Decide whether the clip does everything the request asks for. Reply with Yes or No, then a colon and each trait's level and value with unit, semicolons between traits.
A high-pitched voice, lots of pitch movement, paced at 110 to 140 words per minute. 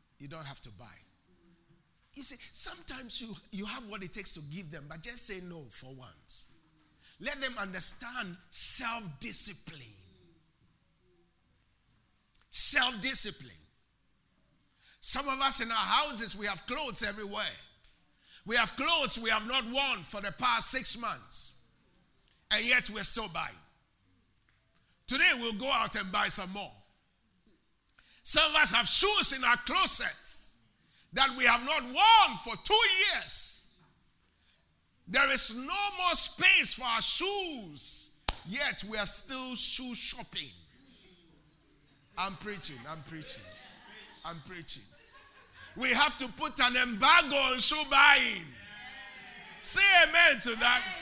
Yes: high, 230 Hz; wide, 7.5 semitones; slow, 135 wpm